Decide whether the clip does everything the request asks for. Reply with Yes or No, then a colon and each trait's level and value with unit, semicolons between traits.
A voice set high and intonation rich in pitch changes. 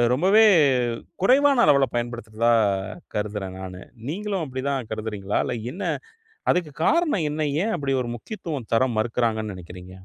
No: low, 125 Hz; wide, 8.7 semitones